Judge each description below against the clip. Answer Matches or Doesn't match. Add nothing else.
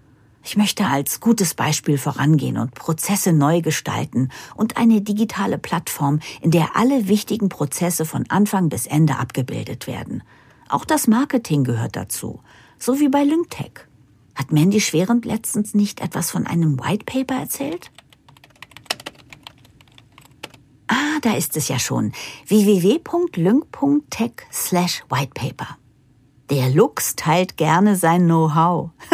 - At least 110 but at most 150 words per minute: Matches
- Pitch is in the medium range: Matches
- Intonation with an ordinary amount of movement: Doesn't match